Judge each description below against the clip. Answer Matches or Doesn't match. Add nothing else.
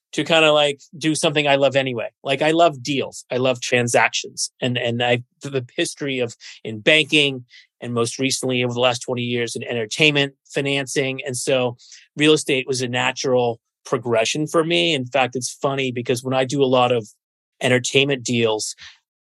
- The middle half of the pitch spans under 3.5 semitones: Matches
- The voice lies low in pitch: Matches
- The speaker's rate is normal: Matches